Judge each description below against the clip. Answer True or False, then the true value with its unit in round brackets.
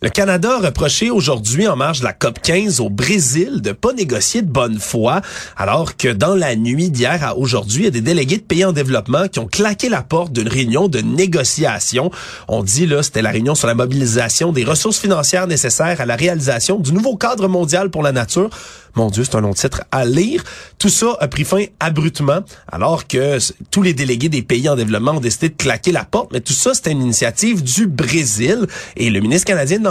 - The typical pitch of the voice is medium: True (155 Hz)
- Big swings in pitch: True (7.2 semitones)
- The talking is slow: False (220 wpm)